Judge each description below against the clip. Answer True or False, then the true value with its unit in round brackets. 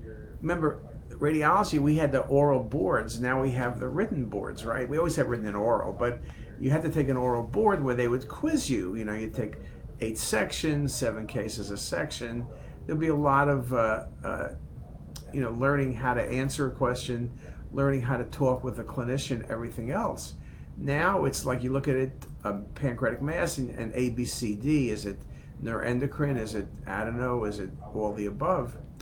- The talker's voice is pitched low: True (130 Hz)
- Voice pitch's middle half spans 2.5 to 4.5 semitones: True (3.3 semitones)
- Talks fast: False (190 wpm)